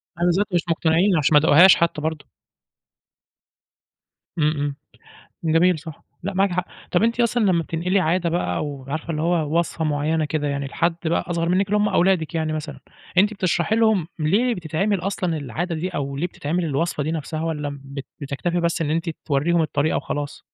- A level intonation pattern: No, average, 3.1 semitones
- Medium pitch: Yes, medium, 165 Hz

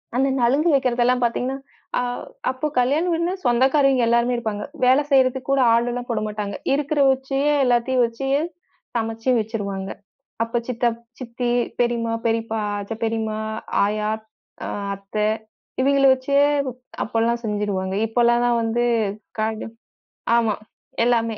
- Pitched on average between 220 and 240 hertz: Yes, high, 235 Hz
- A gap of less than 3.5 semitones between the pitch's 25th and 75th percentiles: Yes, narrow, 2.6 semitones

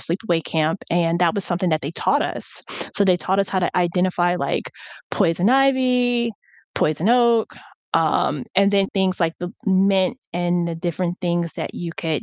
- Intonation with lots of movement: No, average, 2.8 semitones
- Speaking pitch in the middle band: Yes, medium, 180 Hz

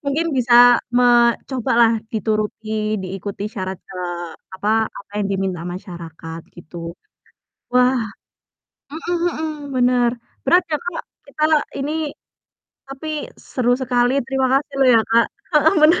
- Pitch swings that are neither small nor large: No, wide, 5.7 semitones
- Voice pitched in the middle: No, high, 240 Hz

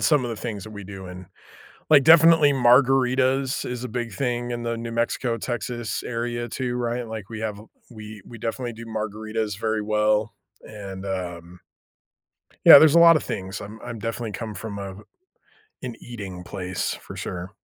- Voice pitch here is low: Yes, low, 115 Hz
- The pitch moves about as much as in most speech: Yes, average, 3.1 semitones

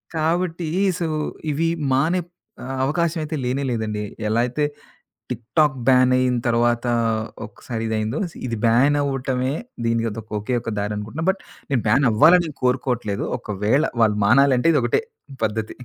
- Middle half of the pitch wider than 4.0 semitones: Yes, average, 4.8 semitones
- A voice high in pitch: No, low, 125 Hz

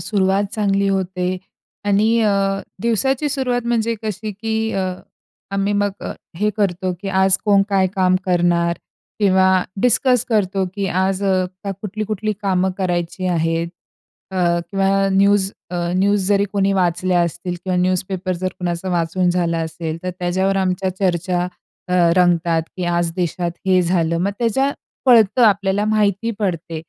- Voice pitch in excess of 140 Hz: Yes, high, 190 Hz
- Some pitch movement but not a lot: No, narrow, 2.3 semitones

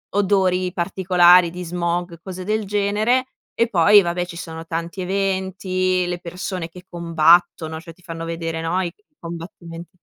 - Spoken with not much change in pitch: Yes, narrow, 2.0 semitones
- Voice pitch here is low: No, medium, 180 Hz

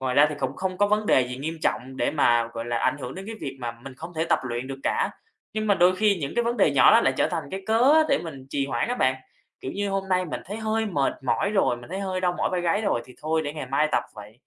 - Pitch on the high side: No, medium, 160 Hz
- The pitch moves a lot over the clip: Yes, wide, 7.0 semitones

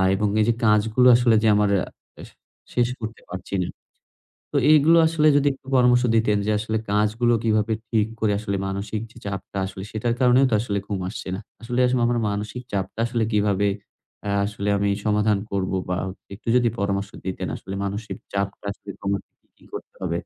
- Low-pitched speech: Yes, low, 105 Hz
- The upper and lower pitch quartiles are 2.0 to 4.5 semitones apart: Yes, average, 2.9 semitones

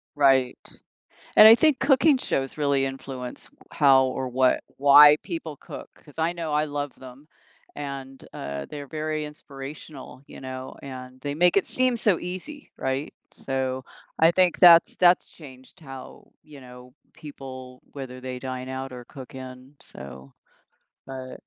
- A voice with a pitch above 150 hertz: No, low, 135 Hz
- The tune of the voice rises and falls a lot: No, average, 3.0 semitones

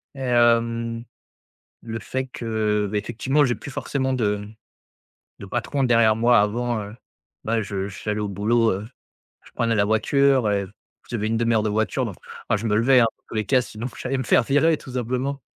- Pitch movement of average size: Yes, average, 3.0 semitones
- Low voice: Yes, low, 115 Hz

